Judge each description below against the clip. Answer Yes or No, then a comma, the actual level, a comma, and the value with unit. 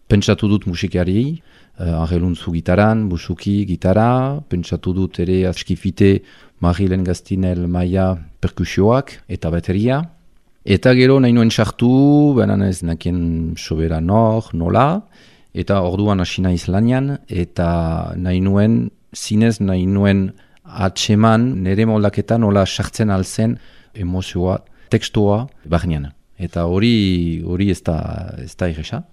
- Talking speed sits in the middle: No, slow, 110 wpm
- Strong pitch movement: No, average, 3.9 semitones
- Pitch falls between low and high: No, very low, 95 Hz